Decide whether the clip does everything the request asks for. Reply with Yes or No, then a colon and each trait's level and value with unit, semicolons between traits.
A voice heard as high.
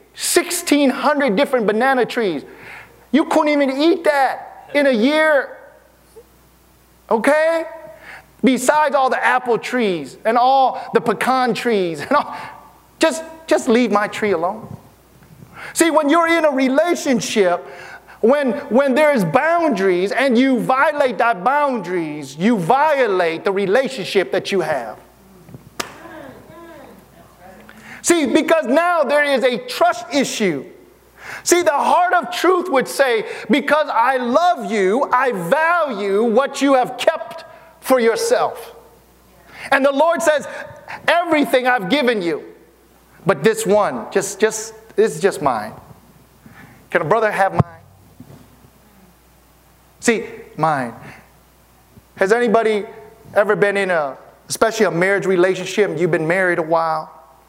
Yes: very high, 255 Hz